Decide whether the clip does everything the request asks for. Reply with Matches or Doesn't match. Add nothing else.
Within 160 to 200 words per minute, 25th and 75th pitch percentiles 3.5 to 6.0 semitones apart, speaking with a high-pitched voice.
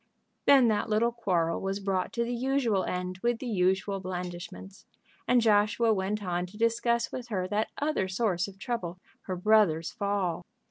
Matches